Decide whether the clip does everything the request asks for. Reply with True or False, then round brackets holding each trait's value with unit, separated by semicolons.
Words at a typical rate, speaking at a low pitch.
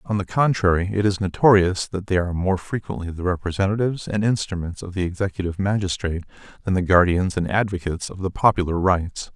True (180 wpm; 95 Hz)